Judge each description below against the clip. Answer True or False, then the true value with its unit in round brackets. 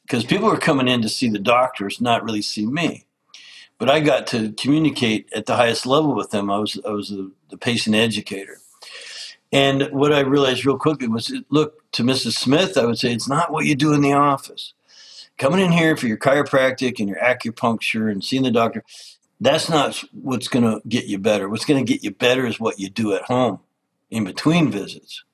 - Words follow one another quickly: True (215 wpm)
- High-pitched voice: False (125 Hz)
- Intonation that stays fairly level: False (4.2 semitones)